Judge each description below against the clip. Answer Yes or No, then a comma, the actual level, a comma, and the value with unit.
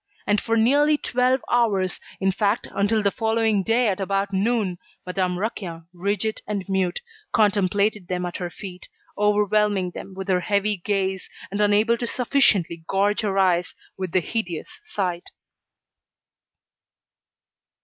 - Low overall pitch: No, high, 200 Hz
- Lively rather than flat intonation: No, average, 2.8 semitones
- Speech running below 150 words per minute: Yes, average, 140 wpm